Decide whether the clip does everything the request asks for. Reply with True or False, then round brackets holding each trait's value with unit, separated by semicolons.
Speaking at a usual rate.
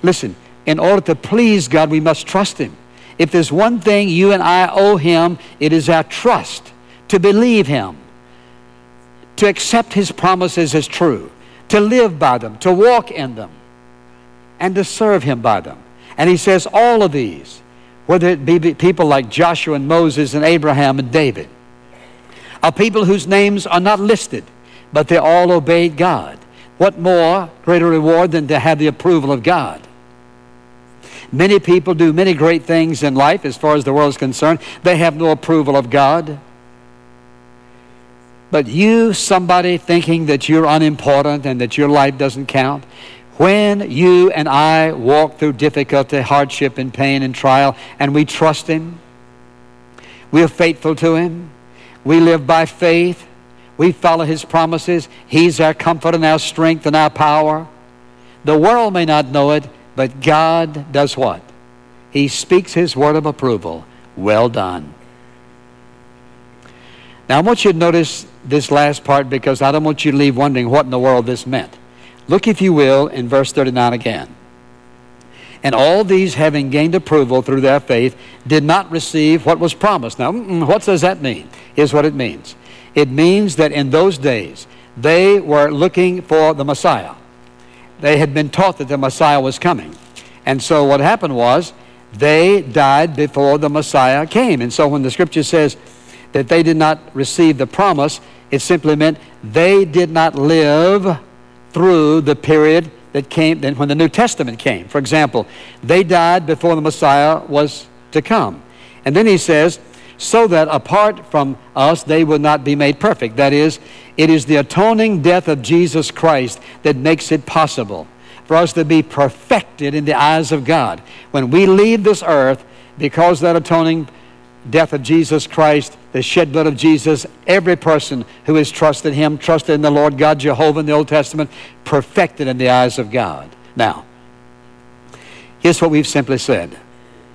True (170 wpm)